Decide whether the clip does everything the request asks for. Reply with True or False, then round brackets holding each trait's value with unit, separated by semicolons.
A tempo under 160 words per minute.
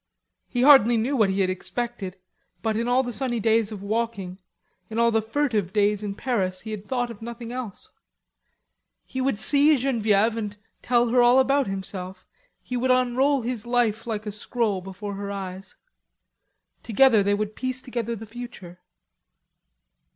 False (165 wpm)